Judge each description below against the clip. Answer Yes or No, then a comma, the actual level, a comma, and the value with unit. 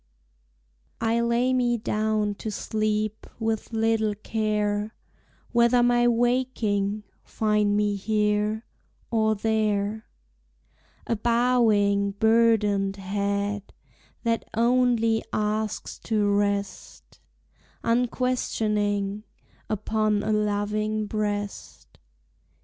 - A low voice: No, high, 215 Hz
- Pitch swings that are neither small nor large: No, narrow, 1.8 semitones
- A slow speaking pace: Yes, slow, 80 wpm